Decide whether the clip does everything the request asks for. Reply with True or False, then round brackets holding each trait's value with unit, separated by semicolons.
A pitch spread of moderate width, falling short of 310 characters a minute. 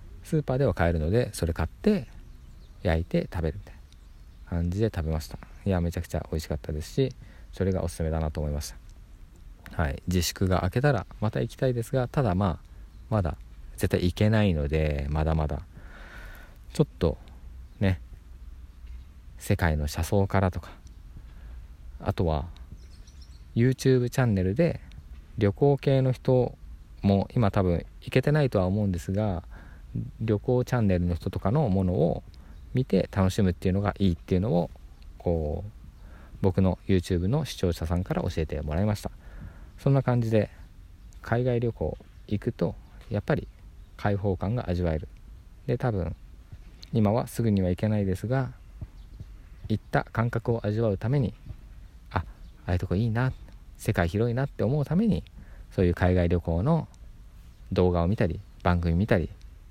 False (4.9 semitones; 315 characters per minute)